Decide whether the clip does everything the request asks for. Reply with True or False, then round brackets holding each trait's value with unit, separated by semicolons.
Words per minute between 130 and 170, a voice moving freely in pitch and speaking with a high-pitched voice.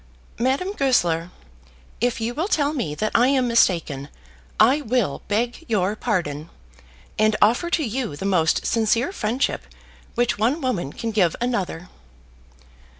True (140 wpm; 5.8 semitones; 225 Hz)